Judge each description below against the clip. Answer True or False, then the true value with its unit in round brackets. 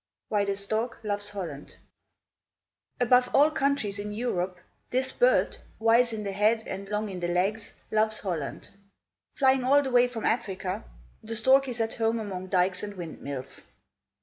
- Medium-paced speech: True (160 wpm)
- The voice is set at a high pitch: True (215 Hz)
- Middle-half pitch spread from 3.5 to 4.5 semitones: True (4.0 semitones)